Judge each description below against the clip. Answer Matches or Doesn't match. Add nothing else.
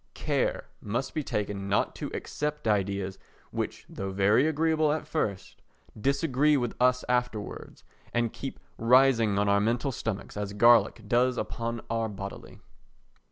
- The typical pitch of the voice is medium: Doesn't match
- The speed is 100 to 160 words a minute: Matches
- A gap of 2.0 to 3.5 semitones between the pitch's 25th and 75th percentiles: Doesn't match